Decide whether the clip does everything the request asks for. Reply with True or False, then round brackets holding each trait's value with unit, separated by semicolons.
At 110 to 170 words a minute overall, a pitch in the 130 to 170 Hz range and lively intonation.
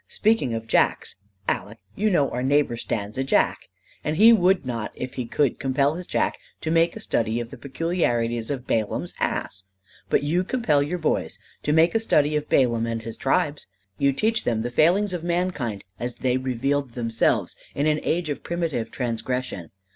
False (185 wpm; 140 Hz; 6.0 semitones)